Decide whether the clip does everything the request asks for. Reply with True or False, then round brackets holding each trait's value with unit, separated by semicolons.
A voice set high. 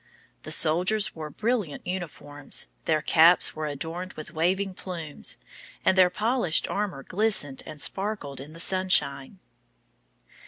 False (170 Hz)